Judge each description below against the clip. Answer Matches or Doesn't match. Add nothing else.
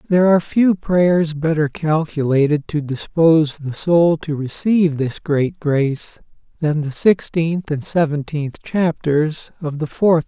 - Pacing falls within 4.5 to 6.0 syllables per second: Doesn't match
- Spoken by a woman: Doesn't match